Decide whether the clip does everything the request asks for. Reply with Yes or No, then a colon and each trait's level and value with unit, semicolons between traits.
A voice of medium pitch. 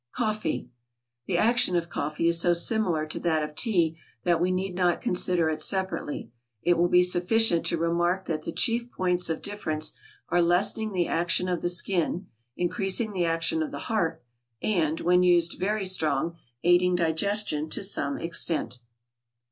Yes: medium, 175 Hz